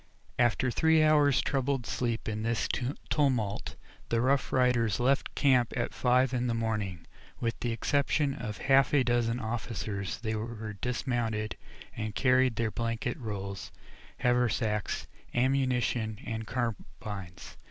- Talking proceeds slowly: Yes, slow, 130 wpm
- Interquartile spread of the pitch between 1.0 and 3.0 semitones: Yes, average, 2.7 semitones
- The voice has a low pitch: Yes, low, 120 Hz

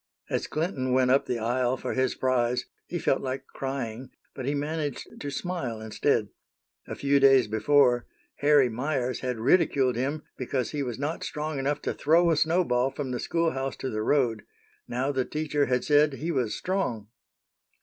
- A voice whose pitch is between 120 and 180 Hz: Yes, low, 135 Hz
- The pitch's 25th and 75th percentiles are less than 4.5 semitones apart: Yes, average, 2.9 semitones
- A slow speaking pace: No, average, 175 wpm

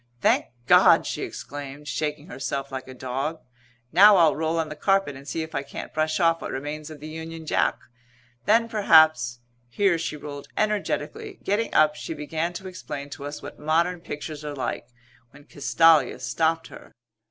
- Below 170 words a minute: No, average, 180 wpm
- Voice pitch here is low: No, medium, 155 Hz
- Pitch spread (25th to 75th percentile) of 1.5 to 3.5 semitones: Yes, average, 2.7 semitones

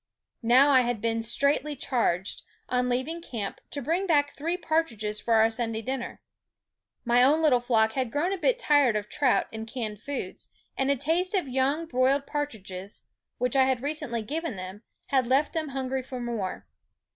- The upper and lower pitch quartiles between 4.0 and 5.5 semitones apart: Yes, average, 4.3 semitones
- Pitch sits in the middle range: No, very high, 255 Hz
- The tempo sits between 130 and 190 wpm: Yes, average, 180 wpm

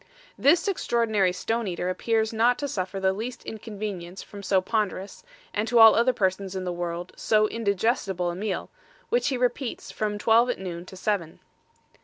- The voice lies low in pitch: No, high, 210 Hz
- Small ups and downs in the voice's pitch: No, average, 3.7 semitones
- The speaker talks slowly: No, average, 175 wpm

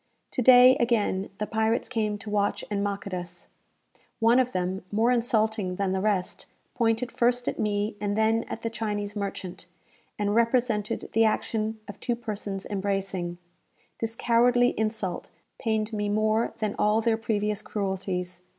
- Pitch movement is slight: Yes, narrow, 2.2 semitones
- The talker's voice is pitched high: Yes, high, 215 Hz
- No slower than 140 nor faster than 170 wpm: Yes, average, 160 wpm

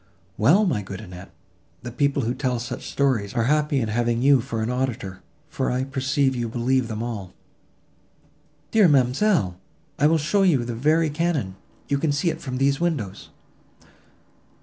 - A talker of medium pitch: No, low, 130 Hz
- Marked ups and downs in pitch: No, average, 4.1 semitones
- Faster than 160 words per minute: Yes, average, 170 wpm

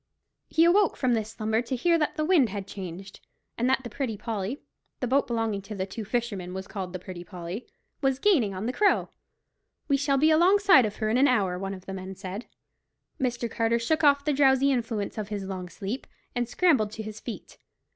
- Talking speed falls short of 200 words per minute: No, fast, 205 wpm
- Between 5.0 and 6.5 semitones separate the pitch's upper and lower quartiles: Yes, wide, 5.6 semitones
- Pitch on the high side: Yes, high, 230 Hz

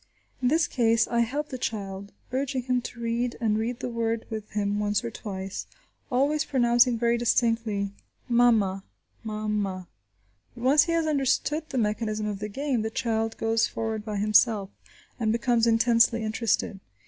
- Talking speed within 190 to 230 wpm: No, average, 160 wpm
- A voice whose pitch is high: Yes, high, 230 Hz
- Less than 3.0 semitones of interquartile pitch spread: Yes, narrow, 2.5 semitones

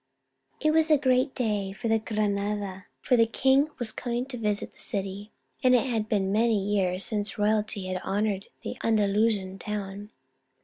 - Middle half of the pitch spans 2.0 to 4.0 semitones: Yes, average, 2.9 semitones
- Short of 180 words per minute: Yes, average, 165 wpm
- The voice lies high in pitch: Yes, high, 210 Hz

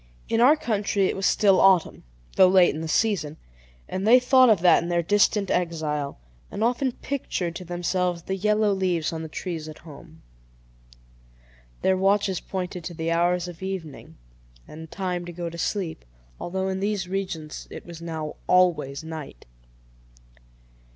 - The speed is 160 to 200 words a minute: Yes, average, 165 wpm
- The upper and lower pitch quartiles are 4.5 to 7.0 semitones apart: No, average, 3.0 semitones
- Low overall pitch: No, medium, 180 Hz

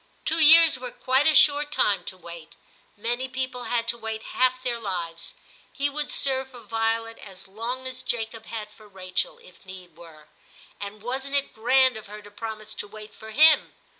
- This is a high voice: Yes, high, 225 Hz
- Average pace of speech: Yes, average, 190 wpm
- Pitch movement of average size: Yes, average, 4.0 semitones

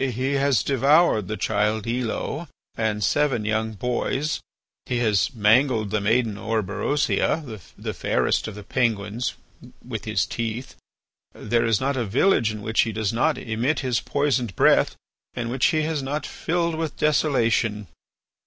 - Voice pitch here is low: Yes, low, 115 Hz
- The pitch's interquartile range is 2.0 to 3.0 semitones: No, average, 4.3 semitones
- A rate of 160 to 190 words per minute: No, average, 150 wpm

